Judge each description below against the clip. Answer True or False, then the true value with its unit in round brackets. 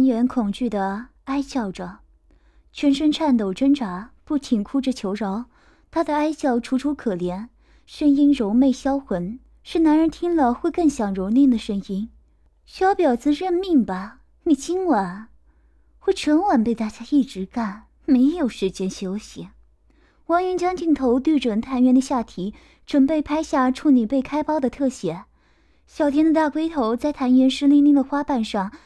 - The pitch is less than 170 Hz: False (265 Hz)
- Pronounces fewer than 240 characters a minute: True (230 characters per minute)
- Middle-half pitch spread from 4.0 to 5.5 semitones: True (5.1 semitones)